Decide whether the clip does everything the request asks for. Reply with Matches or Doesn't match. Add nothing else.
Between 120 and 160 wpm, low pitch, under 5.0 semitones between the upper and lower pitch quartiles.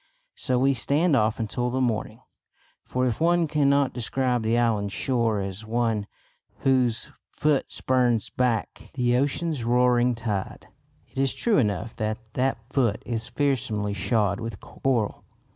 Matches